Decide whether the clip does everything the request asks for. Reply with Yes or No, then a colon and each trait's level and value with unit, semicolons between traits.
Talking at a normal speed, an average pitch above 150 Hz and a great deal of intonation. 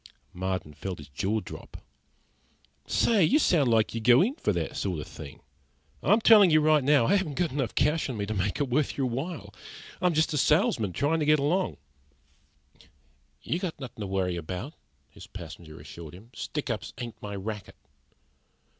No: average, 180 wpm; low, 125 Hz; wide, 7.8 semitones